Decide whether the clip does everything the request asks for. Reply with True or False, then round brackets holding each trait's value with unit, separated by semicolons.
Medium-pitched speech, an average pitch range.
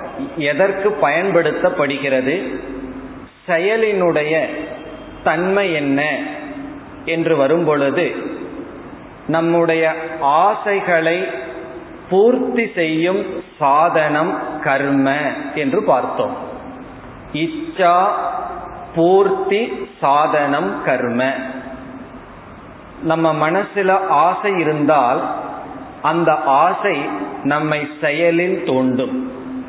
True (165 Hz; 4.6 semitones)